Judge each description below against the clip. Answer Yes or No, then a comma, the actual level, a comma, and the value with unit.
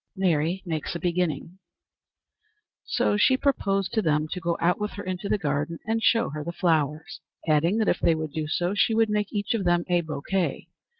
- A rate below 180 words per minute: No, average, 200 wpm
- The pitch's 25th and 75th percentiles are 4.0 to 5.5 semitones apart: Yes, average, 4.3 semitones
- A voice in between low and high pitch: Yes, medium, 175 Hz